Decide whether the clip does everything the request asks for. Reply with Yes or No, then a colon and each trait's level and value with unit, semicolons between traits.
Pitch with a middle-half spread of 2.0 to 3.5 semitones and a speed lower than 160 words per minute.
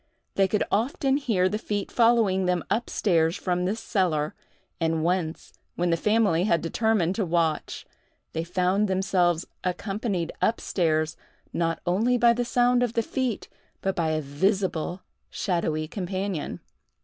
No: average, 4.3 semitones; average, 150 wpm